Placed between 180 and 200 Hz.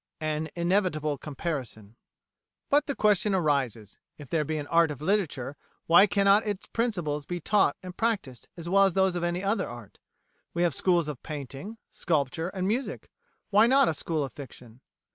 No: medium, 170 Hz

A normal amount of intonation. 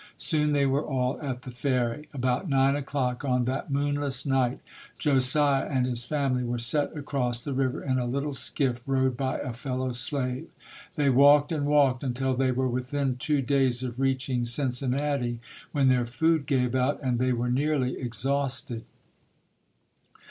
No: narrow, 2.1 semitones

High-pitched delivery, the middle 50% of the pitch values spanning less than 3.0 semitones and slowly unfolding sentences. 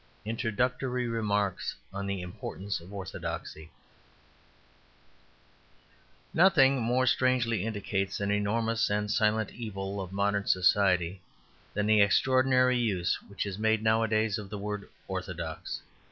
No: low, 105 Hz; narrow, 2.6 semitones; slow, 115 wpm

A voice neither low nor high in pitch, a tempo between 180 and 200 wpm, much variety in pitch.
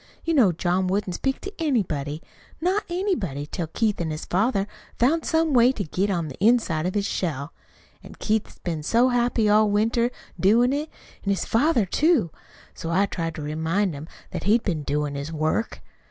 No: high, 200 Hz; average, 185 wpm; wide, 6.8 semitones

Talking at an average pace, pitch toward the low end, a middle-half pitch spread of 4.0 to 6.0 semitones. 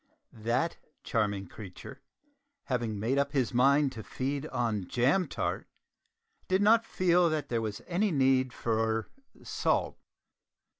No: slow, 130 wpm; low, 130 Hz; average, 5.3 semitones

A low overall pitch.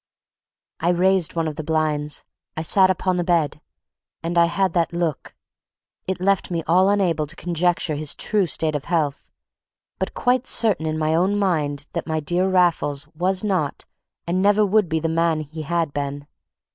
No: medium, 170 Hz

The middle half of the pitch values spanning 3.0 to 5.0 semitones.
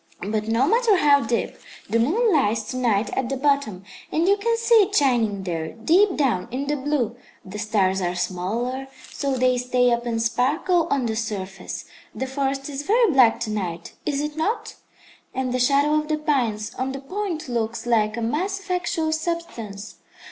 No: wide, 5.5 semitones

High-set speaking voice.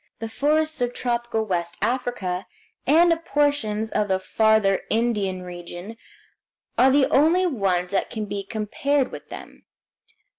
Yes: high, 220 Hz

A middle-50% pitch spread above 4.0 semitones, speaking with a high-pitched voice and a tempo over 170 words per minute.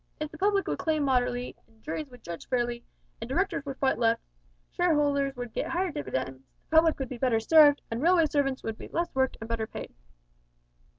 Yes: average, 4.7 semitones; very high, 270 Hz; average, 200 wpm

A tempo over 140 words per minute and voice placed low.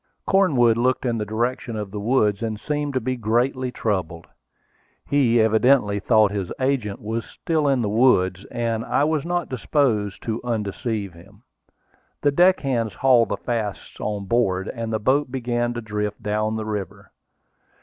Yes: average, 160 wpm; low, 115 Hz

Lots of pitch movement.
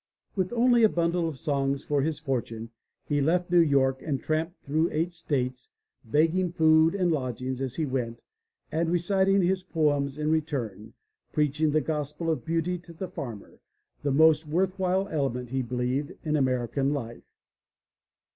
No: average, 4.0 semitones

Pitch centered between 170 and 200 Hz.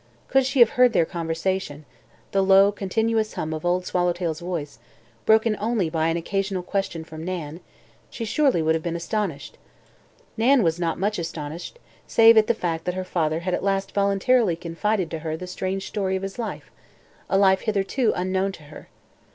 Yes: medium, 185 Hz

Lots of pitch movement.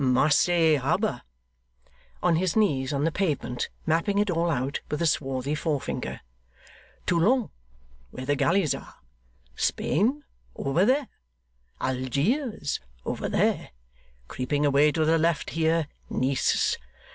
No: average, 4.3 semitones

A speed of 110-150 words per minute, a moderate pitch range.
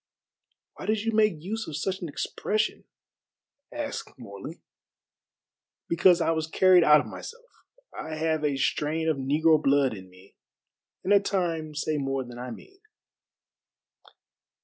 Yes: average, 145 wpm; average, 5.0 semitones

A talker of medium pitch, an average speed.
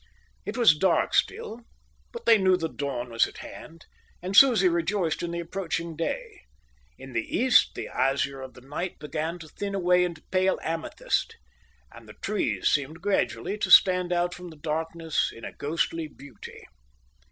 Yes: medium, 170 Hz; average, 170 wpm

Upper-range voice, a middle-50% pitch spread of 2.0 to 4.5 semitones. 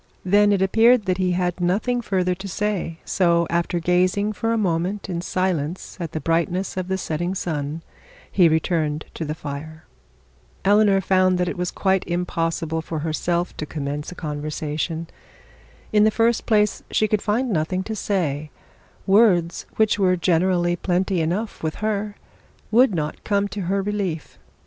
No: medium, 180 Hz; average, 3.6 semitones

